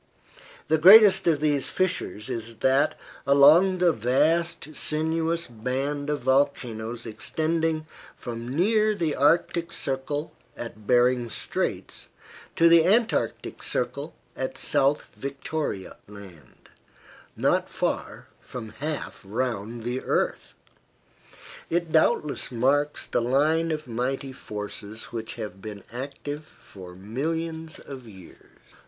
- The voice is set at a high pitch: No, medium, 140 Hz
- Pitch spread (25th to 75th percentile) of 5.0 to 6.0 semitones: Yes, wide, 5.4 semitones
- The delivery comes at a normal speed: No, slow, 110 wpm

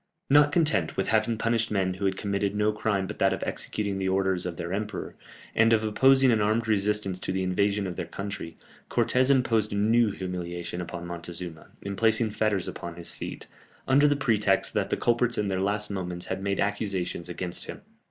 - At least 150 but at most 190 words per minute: No, average, 200 wpm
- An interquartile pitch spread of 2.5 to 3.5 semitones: Yes, average, 3.1 semitones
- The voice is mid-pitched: No, low, 100 Hz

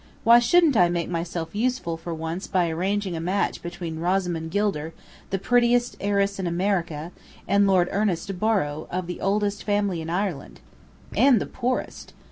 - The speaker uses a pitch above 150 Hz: Yes, high, 190 Hz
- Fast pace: No, average, 160 wpm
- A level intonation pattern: No, average, 3.4 semitones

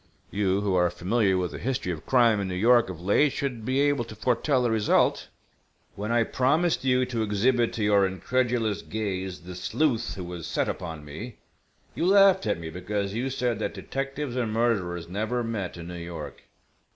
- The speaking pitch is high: No, low, 110 Hz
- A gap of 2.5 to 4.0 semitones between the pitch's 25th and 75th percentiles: No, average, 5.1 semitones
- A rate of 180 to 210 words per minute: Yes, average, 190 wpm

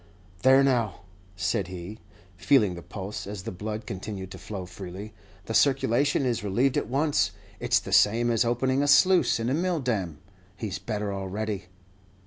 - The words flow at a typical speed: Yes, average, 170 wpm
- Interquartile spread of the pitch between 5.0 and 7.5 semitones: Yes, average, 5.3 semitones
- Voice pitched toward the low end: Yes, low, 110 Hz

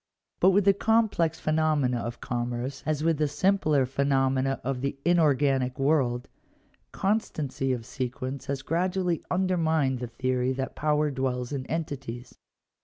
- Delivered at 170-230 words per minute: No, average, 140 wpm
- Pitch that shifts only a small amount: No, average, 3.9 semitones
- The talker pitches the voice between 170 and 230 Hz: No, medium, 140 Hz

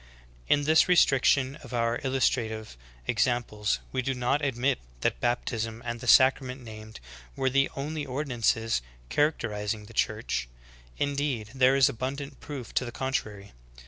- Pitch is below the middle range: Yes, low, 125 Hz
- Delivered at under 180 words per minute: Yes, average, 140 wpm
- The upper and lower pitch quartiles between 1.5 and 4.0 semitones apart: Yes, average, 3.5 semitones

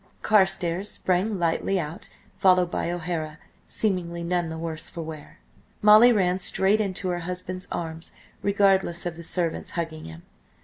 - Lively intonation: No, narrow, 2.5 semitones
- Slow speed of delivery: No, average, 145 wpm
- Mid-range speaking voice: Yes, medium, 175 Hz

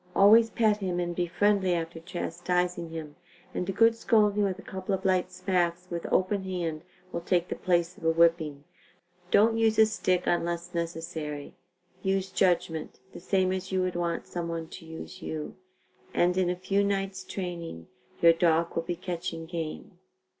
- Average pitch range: No, narrow, 2.2 semitones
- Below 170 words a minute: No, average, 175 wpm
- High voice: No, medium, 175 Hz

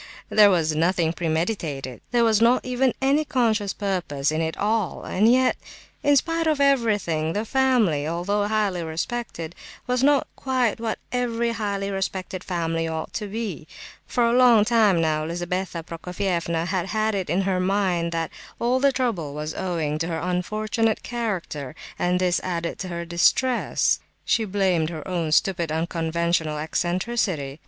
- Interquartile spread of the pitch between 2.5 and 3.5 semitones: No, wide, 5.4 semitones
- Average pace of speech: Yes, average, 155 wpm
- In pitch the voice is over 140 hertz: Yes, medium, 185 Hz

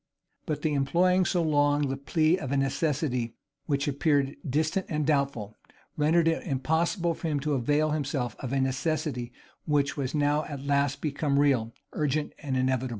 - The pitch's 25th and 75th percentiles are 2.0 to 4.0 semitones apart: Yes, narrow, 2.4 semitones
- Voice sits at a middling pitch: Yes, medium, 145 Hz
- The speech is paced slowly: No, average, 165 wpm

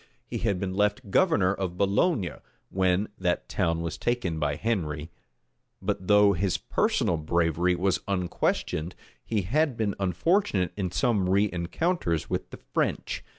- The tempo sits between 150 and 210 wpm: No, average, 140 wpm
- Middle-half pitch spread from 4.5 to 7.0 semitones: No, average, 3.1 semitones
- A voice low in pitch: Yes, very low, 95 Hz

